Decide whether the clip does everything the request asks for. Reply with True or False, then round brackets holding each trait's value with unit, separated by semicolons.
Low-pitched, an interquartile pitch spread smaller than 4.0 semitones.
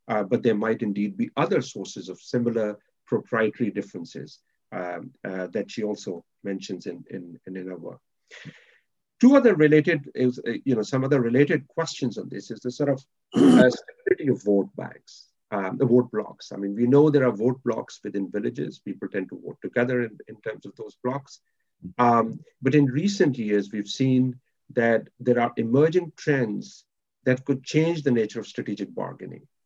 False (125 Hz; 5.0 semitones)